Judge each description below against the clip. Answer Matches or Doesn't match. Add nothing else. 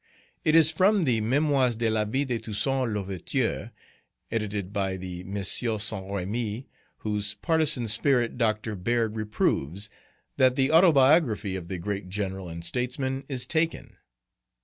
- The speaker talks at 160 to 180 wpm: Doesn't match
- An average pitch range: Matches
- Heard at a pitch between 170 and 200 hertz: Doesn't match